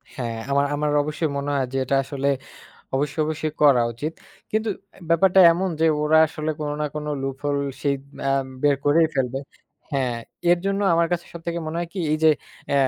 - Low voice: No, medium, 150 Hz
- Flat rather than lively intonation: No, average, 3.2 semitones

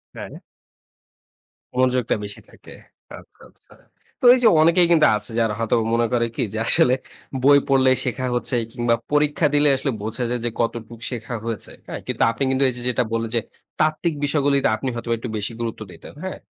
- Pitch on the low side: Yes, low, 125 Hz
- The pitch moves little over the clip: No, average, 3.6 semitones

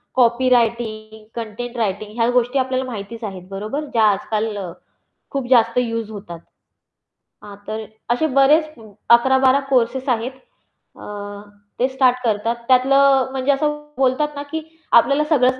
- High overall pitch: Yes, high, 245 Hz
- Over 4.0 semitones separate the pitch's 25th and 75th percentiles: No, average, 3.1 semitones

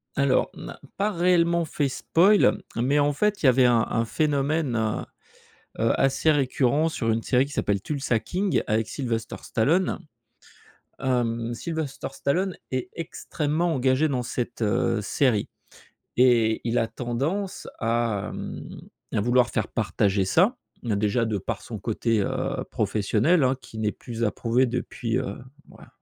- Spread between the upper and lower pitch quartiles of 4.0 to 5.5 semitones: Yes, average, 4.7 semitones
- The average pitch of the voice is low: Yes, low, 125 Hz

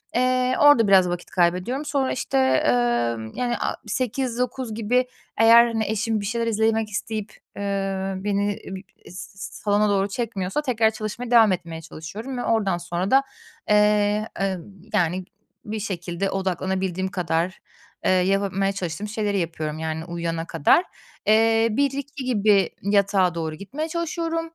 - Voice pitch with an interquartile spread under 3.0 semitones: No, average, 4.1 semitones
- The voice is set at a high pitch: Yes, high, 205 Hz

